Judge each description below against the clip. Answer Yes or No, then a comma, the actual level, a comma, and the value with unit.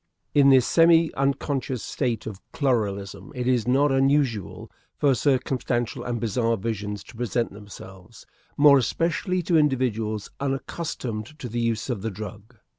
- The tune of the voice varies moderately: Yes, average, 4.2 semitones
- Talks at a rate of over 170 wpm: No, average, 140 wpm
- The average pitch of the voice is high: No, low, 125 Hz